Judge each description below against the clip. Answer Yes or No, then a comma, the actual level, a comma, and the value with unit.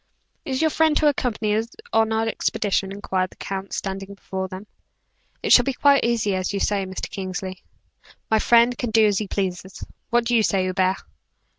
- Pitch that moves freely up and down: No, average, 3.6 semitones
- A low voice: No, high, 205 Hz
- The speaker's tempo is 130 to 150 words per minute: No, average, 185 wpm